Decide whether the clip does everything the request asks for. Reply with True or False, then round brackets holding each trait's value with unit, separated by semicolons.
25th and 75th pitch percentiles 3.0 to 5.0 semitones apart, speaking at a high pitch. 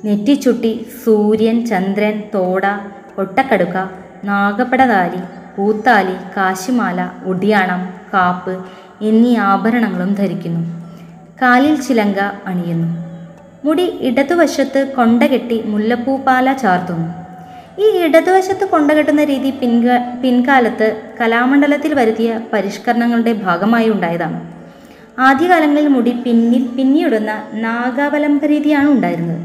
False (5.4 semitones; 225 Hz)